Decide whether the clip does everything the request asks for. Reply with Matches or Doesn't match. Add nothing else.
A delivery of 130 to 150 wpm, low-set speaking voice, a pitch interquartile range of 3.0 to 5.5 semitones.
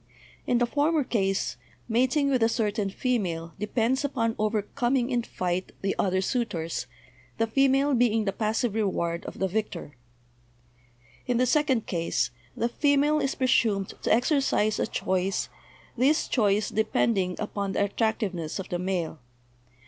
Doesn't match